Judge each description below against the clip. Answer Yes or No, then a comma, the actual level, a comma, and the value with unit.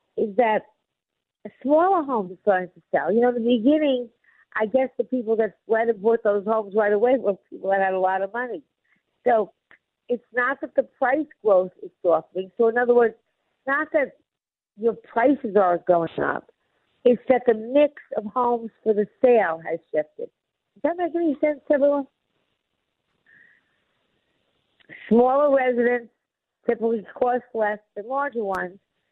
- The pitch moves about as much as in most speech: Yes, average, 4.2 semitones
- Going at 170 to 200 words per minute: No, average, 160 wpm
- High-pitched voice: Yes, high, 235 Hz